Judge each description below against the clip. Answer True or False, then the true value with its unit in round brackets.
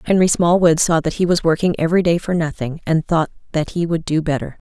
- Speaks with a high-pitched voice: False (165 Hz)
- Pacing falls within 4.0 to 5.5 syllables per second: False (6.1 syllables/s)